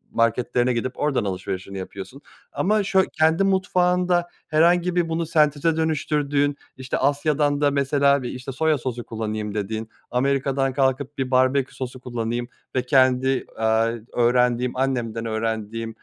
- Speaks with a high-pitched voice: No, low, 130 Hz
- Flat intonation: No, average, 4.1 semitones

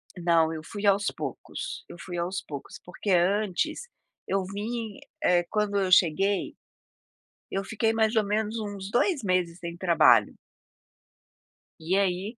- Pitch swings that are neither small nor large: Yes, average, 3.2 semitones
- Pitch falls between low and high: No, high, 195 Hz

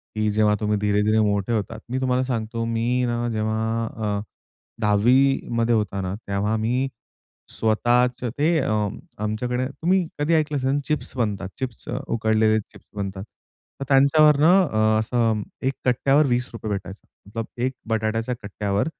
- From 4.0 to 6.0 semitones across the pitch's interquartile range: No, average, 3.2 semitones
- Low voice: Yes, low, 115 Hz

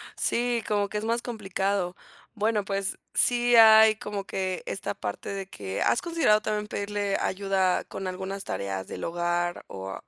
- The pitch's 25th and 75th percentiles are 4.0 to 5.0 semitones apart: No, average, 2.8 semitones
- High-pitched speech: Yes, high, 200 Hz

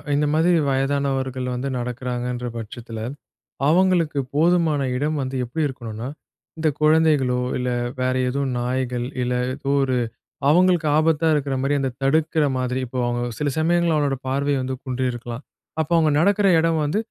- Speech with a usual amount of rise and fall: Yes, average, 3.8 semitones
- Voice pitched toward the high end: No, medium, 140 Hz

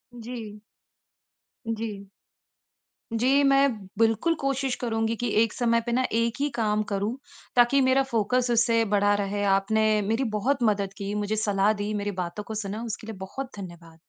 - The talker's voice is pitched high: Yes, high, 225 Hz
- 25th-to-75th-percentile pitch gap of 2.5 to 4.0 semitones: Yes, average, 2.9 semitones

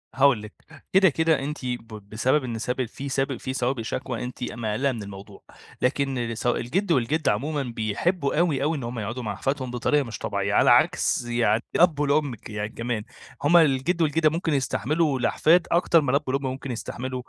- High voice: No, low, 130 Hz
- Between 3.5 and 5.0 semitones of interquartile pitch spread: Yes, average, 3.8 semitones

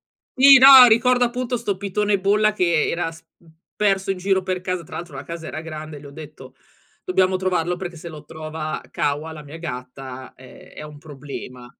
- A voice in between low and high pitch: Yes, medium, 170 Hz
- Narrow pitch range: No, average, 4.6 semitones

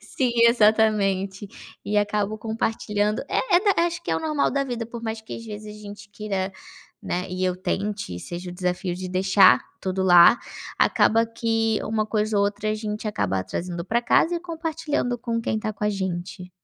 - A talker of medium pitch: No, high, 210 Hz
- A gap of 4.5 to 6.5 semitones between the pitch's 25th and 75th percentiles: No, average, 3.2 semitones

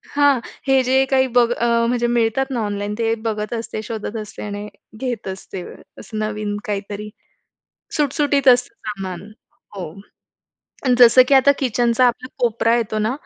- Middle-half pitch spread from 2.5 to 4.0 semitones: Yes, average, 3.2 semitones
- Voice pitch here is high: Yes, high, 230 Hz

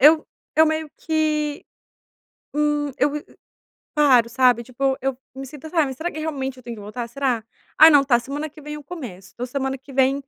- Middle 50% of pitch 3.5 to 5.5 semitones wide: No, average, 3.0 semitones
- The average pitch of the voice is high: Yes, very high, 275 Hz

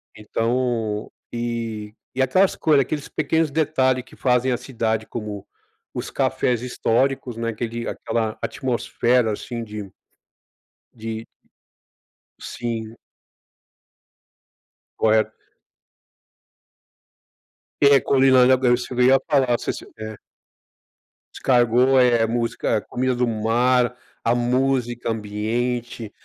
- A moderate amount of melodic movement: No, narrow, 2.3 semitones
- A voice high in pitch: No, low, 120 Hz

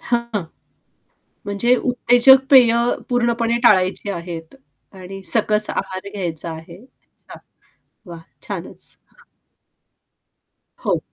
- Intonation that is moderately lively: Yes, average, 4.6 semitones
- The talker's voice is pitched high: Yes, high, 210 Hz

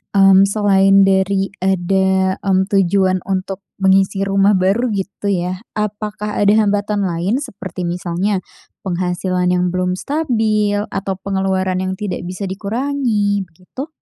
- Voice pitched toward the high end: Yes, high, 195 Hz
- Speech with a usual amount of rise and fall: No, narrow, 1.6 semitones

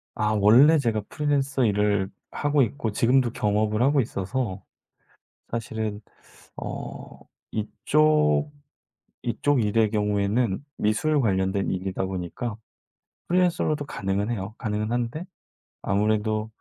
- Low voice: Yes, low, 110 Hz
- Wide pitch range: No, average, 4.5 semitones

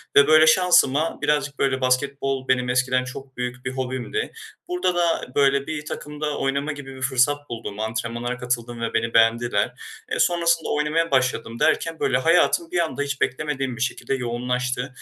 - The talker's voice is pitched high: No, low, 135 Hz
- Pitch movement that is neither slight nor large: Yes, average, 3.1 semitones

